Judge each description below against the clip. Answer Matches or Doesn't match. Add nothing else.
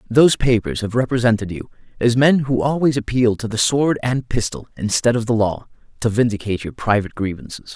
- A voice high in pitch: Doesn't match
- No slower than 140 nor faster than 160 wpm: Doesn't match